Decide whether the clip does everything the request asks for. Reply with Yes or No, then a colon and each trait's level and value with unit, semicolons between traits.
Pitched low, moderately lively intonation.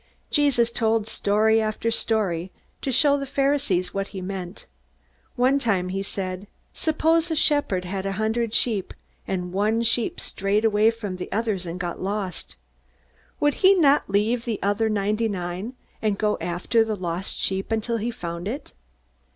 No: high, 215 Hz; average, 3.6 semitones